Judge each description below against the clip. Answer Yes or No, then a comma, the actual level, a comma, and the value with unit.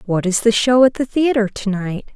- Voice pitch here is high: Yes, high, 225 Hz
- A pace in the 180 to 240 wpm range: No, fast, 250 wpm